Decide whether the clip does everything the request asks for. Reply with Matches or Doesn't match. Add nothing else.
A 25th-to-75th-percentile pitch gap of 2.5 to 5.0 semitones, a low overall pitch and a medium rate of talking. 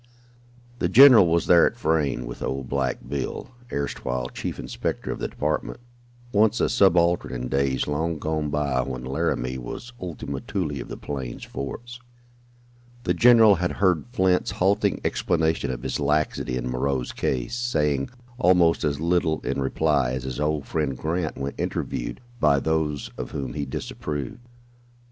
Matches